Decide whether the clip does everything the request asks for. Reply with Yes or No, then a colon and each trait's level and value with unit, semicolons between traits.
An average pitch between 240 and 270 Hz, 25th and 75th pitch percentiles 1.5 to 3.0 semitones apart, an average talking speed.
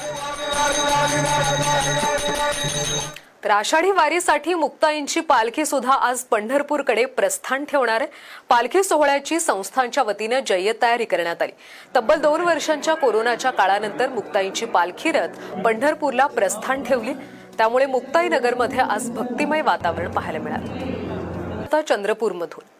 No: very high, 260 Hz; wide, 5.5 semitones; average, 90 wpm